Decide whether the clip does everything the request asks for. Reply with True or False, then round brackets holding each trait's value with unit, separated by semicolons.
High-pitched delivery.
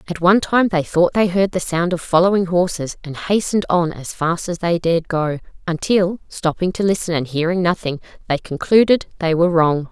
False (175 Hz)